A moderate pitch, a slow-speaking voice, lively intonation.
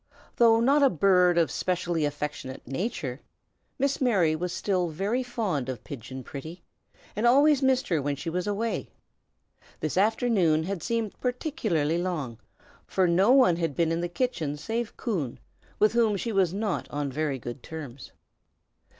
No: medium, 180 Hz; average, 160 wpm; wide, 6.8 semitones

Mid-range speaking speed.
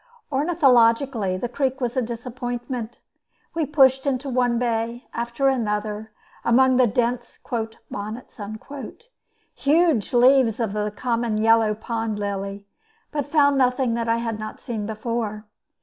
No: slow, 130 wpm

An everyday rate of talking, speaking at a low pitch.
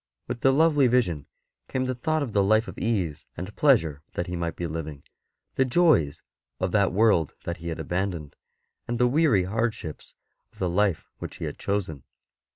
Yes: average, 180 wpm; low, 100 Hz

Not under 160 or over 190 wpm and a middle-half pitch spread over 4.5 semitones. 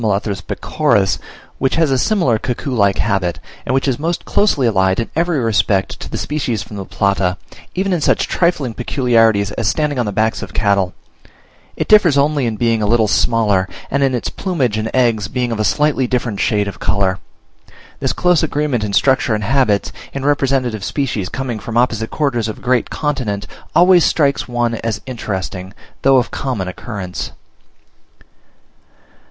Yes: average, 170 wpm; average, 5.1 semitones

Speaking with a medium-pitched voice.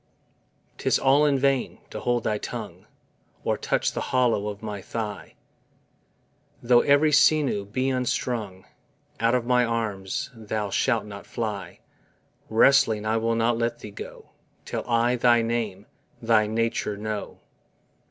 No: low, 115 Hz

